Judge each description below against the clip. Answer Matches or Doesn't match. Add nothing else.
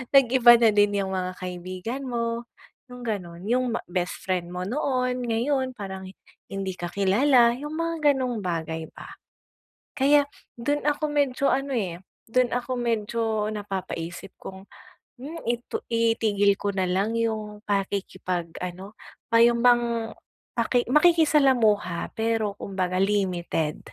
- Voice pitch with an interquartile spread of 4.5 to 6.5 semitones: Matches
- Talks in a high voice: Matches